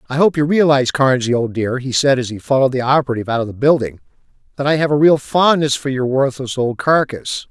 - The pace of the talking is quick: Yes, fast, 230 wpm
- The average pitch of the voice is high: No, low, 135 Hz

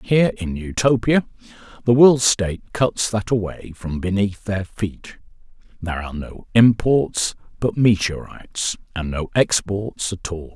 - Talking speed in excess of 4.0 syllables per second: Yes, 4.3 syllables/s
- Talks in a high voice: No, low, 105 Hz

